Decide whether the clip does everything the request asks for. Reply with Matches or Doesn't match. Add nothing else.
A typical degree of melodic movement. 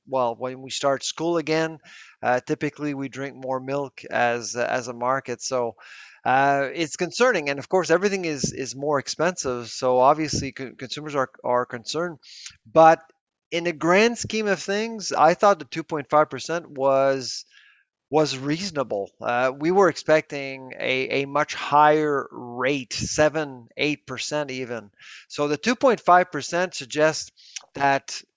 Matches